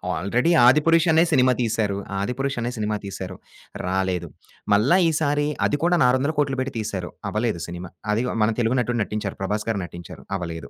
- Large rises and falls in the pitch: Yes, wide, 6.0 semitones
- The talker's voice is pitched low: Yes, low, 115 Hz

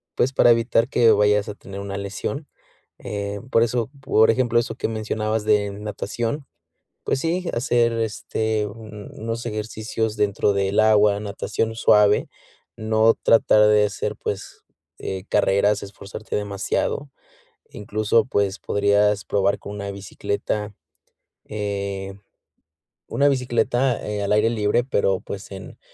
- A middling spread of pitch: No, narrow, 2.0 semitones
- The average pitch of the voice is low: Yes, low, 105 Hz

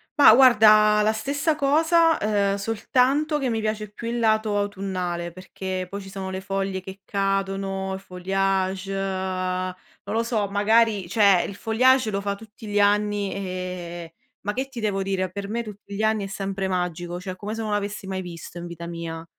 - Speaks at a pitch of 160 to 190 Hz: No, high, 200 Hz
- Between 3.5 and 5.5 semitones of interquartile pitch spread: No, narrow, 2.4 semitones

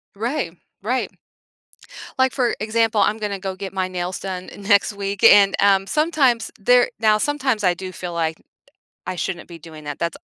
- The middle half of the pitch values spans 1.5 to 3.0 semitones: No, average, 3.7 semitones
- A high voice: Yes, high, 200 Hz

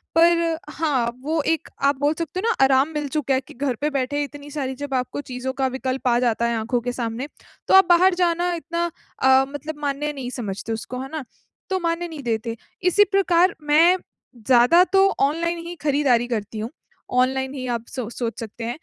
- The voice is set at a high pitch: Yes, very high, 280 Hz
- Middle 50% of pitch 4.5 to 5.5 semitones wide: Yes, average, 4.8 semitones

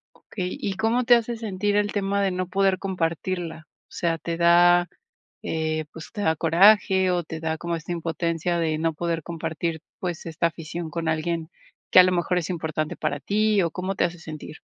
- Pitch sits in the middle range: Yes, medium, 170 Hz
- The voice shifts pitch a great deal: No, narrow, 2.6 semitones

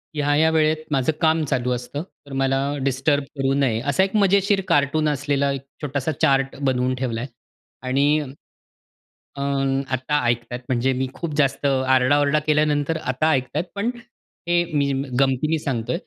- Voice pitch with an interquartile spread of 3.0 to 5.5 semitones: No, narrow, 2.6 semitones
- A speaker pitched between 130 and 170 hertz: Yes, medium, 140 Hz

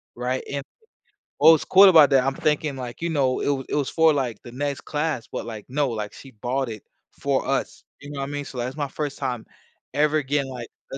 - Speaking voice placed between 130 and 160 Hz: Yes, low, 135 Hz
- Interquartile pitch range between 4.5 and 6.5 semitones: No, average, 2.7 semitones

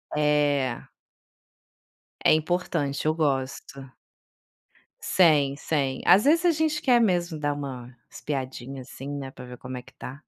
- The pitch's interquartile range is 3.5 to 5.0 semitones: Yes, average, 4.0 semitones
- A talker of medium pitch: Yes, medium, 145 Hz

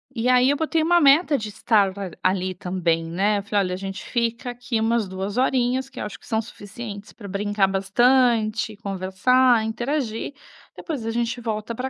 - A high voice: Yes, high, 220 Hz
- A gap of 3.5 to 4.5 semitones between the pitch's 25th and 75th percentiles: Yes, average, 4.0 semitones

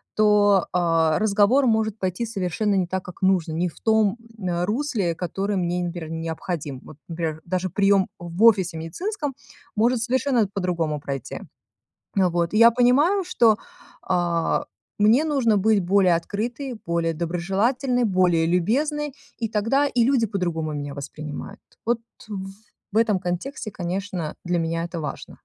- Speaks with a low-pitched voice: No, high, 190 Hz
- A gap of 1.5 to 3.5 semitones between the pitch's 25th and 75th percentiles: No, average, 4.9 semitones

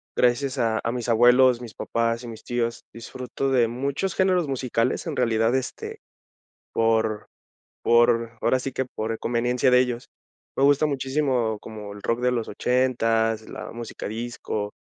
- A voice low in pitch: Yes, low, 120 Hz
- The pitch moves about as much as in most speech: No, narrow, 2.1 semitones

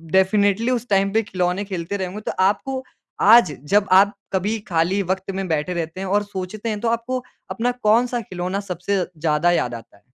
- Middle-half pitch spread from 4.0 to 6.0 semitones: No, average, 3.2 semitones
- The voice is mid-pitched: No, high, 195 Hz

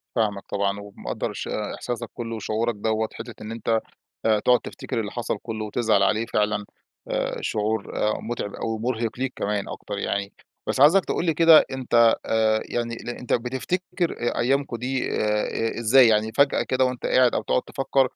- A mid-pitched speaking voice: No, low, 115 Hz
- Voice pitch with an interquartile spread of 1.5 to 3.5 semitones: Yes, average, 2.9 semitones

